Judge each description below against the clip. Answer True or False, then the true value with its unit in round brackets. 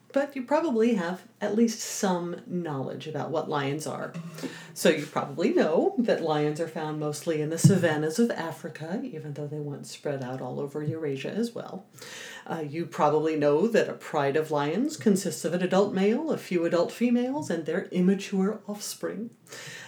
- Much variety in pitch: True (6.0 semitones)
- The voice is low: False (170 Hz)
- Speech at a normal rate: True (180 wpm)